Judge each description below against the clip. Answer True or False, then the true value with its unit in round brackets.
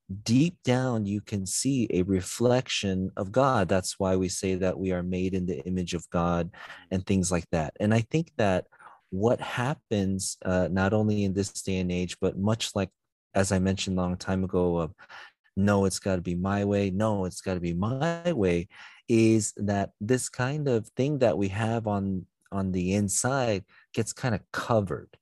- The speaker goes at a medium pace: True (195 wpm)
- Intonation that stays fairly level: False (3.0 semitones)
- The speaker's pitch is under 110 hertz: True (95 Hz)